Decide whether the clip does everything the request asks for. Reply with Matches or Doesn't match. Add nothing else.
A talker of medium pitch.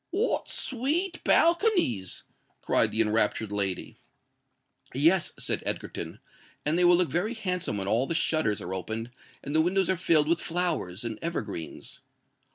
Matches